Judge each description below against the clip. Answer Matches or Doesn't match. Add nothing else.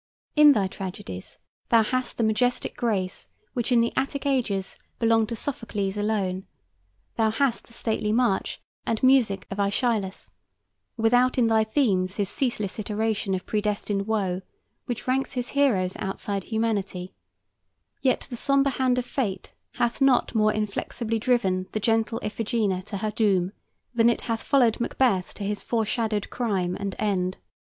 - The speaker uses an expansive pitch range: Doesn't match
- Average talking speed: Matches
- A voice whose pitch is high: Matches